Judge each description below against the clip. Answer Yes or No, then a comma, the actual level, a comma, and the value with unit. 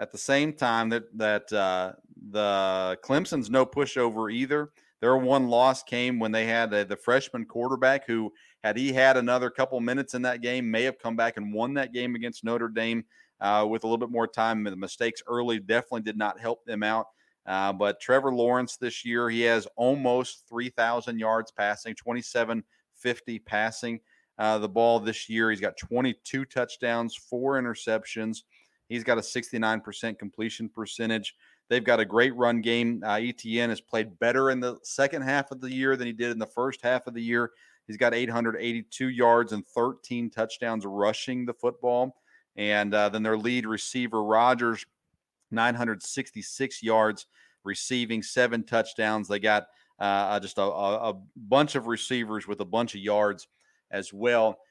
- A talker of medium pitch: No, low, 115 Hz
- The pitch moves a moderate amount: No, narrow, 2.0 semitones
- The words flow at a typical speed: Yes, average, 175 wpm